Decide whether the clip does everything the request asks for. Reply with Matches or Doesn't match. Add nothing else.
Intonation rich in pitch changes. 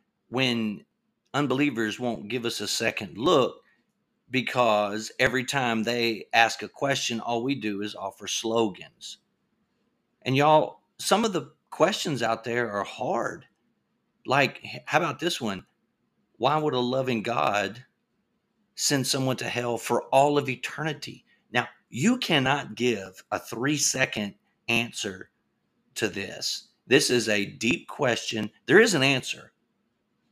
Doesn't match